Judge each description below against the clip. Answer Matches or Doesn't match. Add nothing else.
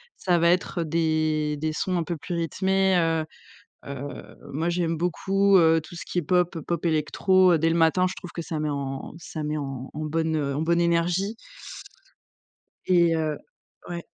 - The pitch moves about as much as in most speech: Doesn't match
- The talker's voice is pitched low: Doesn't match